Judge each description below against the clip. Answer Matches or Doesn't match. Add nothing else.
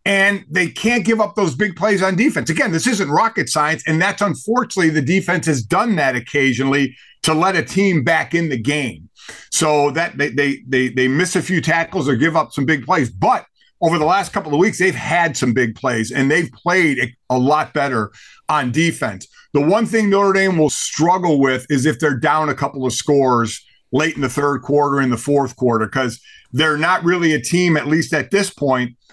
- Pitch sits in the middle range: Matches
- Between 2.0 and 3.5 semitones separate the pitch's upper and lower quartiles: Doesn't match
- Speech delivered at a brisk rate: Matches